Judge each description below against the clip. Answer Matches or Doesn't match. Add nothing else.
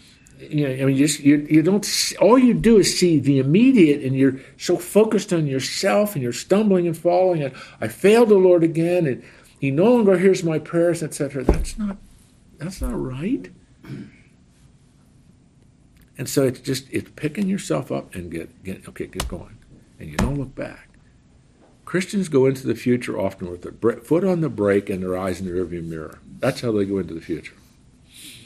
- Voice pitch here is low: Doesn't match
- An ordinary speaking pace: Matches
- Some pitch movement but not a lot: Doesn't match